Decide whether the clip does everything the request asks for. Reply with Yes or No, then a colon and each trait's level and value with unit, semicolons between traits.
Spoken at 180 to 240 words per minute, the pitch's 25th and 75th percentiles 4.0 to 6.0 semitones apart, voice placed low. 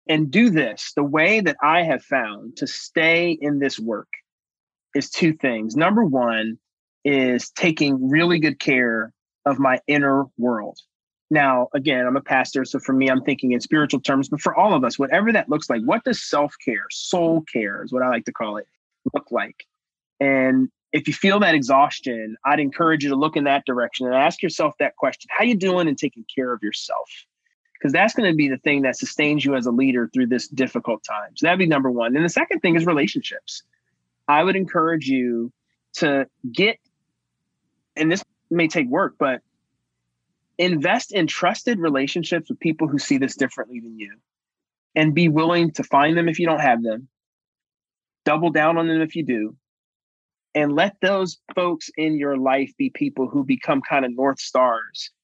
No: average, 195 wpm; average, 4.4 semitones; medium, 145 Hz